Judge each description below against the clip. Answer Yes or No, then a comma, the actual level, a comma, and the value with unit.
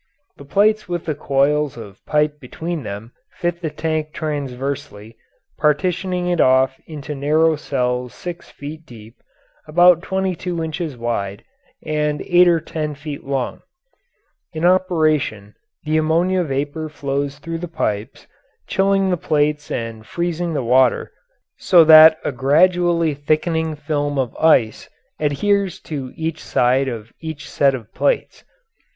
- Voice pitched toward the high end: No, medium, 150 Hz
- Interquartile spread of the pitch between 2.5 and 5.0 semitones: Yes, average, 3.8 semitones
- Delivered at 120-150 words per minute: Yes, average, 140 wpm